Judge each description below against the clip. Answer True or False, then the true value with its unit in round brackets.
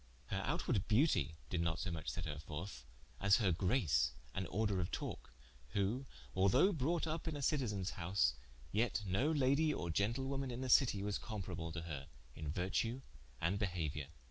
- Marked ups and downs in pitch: True (7.4 semitones)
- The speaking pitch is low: True (100 Hz)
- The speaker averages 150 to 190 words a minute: True (170 wpm)